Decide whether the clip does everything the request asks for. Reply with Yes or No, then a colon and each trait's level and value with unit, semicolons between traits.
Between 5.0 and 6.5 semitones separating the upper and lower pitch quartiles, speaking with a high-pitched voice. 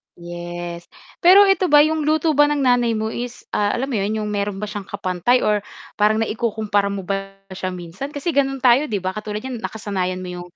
Yes: wide, 5.4 semitones; high, 210 Hz